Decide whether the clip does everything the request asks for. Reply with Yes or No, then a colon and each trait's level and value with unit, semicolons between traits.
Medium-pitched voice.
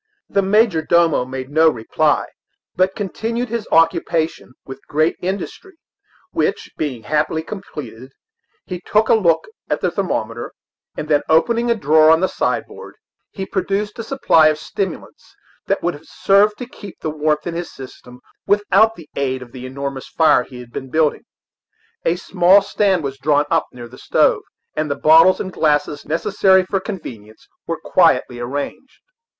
Yes: medium, 160 Hz